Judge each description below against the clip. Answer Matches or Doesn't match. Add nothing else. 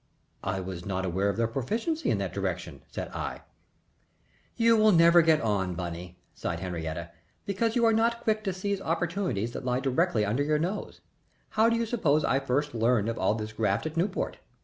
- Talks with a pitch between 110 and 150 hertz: Matches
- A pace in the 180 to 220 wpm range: Matches